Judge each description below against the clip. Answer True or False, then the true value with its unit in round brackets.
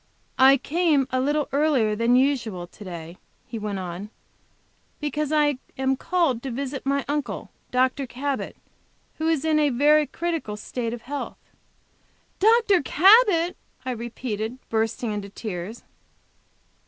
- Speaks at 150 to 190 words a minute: False (135 wpm)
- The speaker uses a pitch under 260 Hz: False (265 Hz)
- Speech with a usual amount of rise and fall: True (5.0 semitones)